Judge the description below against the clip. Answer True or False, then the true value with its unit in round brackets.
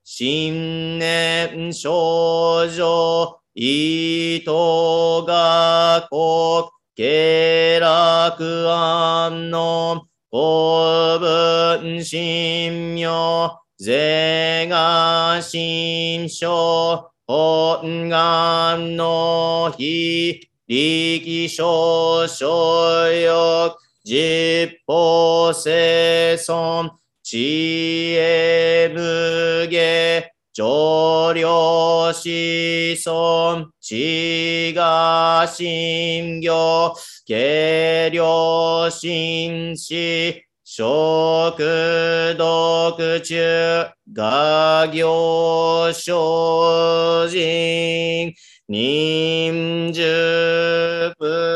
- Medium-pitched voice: True (165 Hz)